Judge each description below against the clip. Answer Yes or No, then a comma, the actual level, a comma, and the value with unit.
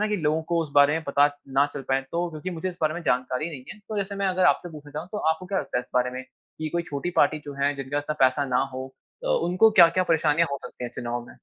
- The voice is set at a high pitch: No, medium, 155 Hz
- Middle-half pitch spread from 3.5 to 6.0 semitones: Yes, average, 4.3 semitones